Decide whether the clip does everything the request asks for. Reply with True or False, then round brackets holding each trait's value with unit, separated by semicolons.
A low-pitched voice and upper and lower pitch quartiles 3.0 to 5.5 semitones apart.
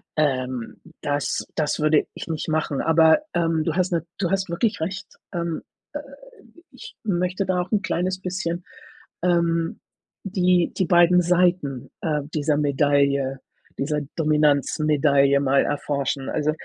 False (160 Hz; 3.7 semitones)